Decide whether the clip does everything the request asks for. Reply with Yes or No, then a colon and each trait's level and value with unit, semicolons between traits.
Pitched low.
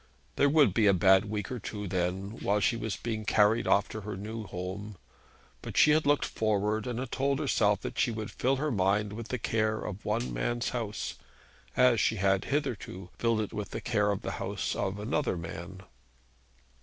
Yes: low, 105 Hz